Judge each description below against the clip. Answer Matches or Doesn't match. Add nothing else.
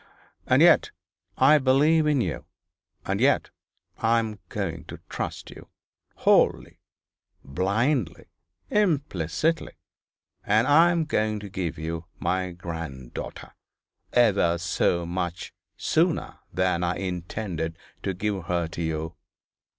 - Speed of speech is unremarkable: Doesn't match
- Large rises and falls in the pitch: Matches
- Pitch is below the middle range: Matches